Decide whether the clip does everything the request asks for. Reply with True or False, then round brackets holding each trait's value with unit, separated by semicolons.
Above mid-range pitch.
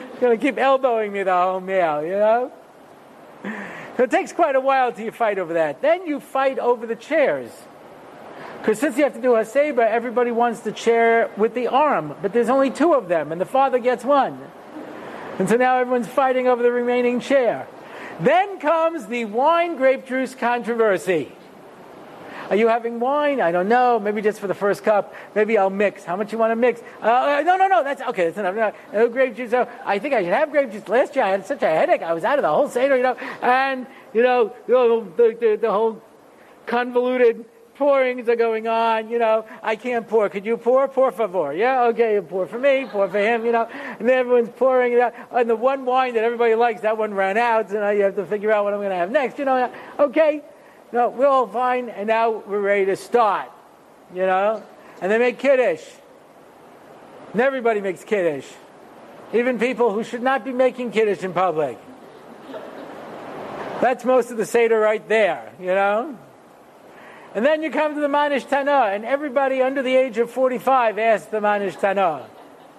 True (240 Hz)